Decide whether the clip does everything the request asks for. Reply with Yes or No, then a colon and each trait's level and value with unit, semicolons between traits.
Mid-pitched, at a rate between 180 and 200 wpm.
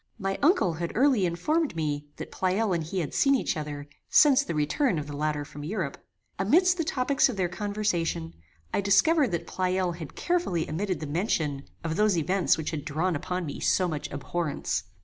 Yes: medium, 180 Hz; average, 190 wpm